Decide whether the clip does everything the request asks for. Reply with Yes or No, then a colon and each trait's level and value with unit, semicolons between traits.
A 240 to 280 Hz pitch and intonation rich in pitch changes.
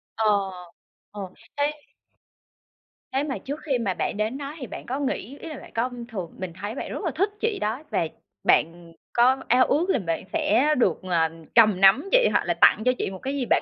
Yes: high, 245 Hz; wide, 6.4 semitones